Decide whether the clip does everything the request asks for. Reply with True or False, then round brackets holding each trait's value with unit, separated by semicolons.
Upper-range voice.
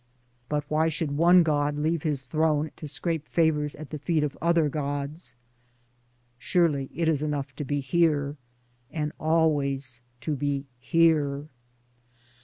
False (150 Hz)